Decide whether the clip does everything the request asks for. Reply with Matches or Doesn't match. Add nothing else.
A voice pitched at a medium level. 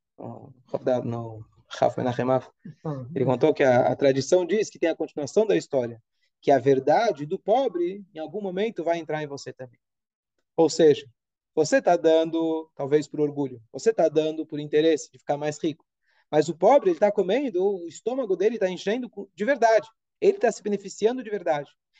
Matches